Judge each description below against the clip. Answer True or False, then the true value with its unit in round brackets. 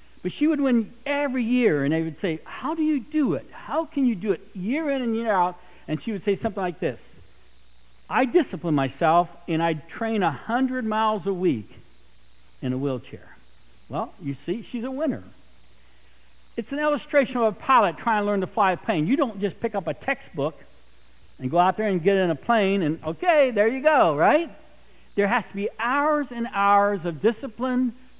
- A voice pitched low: False (205 Hz)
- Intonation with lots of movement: True (8.0 semitones)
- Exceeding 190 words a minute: True (205 wpm)